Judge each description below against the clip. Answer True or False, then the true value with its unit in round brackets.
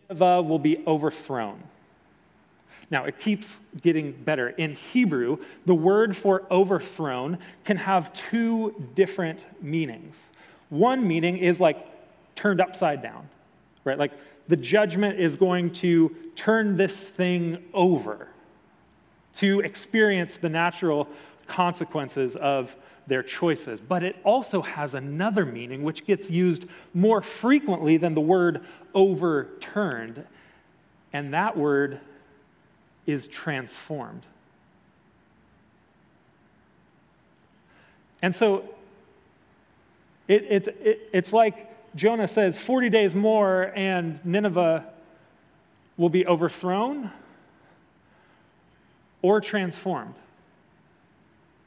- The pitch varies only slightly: False (4.0 semitones)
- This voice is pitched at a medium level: True (180 Hz)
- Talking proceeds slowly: True (100 wpm)